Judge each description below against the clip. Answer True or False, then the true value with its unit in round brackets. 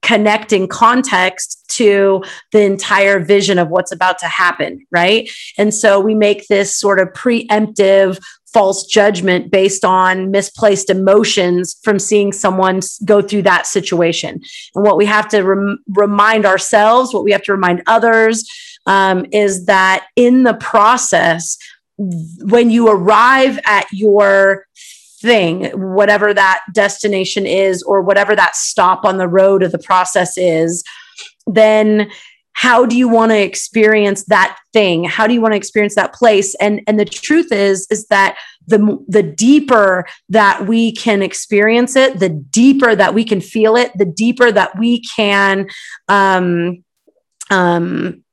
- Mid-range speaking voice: False (205 Hz)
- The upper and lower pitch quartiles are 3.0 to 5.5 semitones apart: False (2.4 semitones)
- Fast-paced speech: False (150 wpm)